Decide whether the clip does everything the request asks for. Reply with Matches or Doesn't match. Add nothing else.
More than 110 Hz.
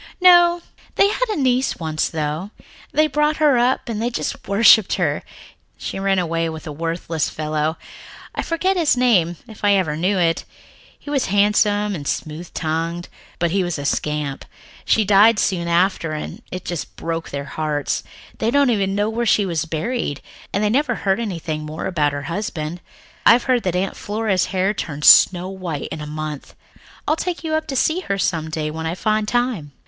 Matches